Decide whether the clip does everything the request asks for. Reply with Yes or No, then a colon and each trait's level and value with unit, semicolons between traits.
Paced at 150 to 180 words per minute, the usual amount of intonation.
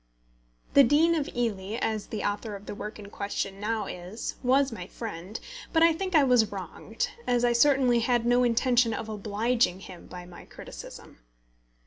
Yes: average, 175 wpm; average, 3.5 semitones